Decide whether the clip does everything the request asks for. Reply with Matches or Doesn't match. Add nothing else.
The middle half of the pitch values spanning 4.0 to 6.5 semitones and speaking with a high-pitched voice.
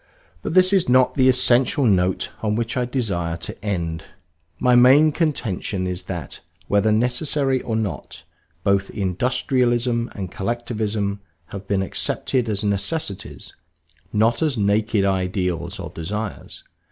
Doesn't match